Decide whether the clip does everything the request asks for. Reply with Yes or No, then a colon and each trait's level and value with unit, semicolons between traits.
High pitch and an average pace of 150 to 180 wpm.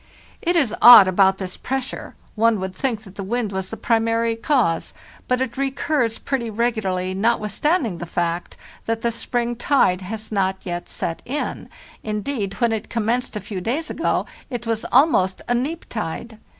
Yes: high, 225 Hz; average, 175 wpm